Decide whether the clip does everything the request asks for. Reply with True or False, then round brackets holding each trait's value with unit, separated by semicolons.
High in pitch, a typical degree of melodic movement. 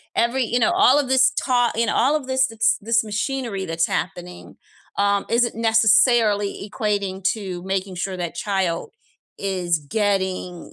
True (205 Hz; 4.1 semitones)